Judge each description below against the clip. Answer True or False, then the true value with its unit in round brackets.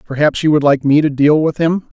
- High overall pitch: False (150 Hz)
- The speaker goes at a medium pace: False (270 wpm)